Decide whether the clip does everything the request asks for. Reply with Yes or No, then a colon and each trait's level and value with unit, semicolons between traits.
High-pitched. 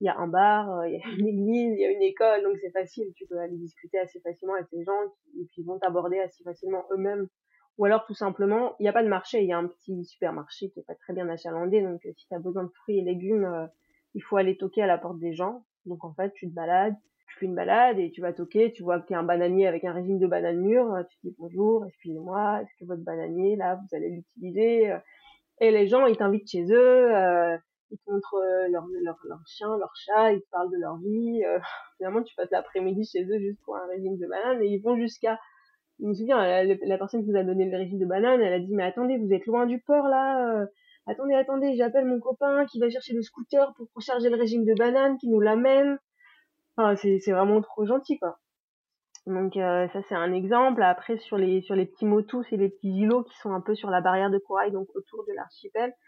Yes: high, 200 Hz